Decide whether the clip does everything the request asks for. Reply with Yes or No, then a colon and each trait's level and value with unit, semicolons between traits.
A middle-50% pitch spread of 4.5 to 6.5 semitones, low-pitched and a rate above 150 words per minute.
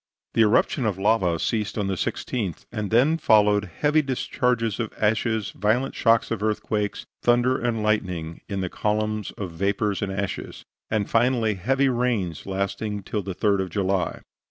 No: average, 2.8 semitones; low, 105 Hz; average, 160 wpm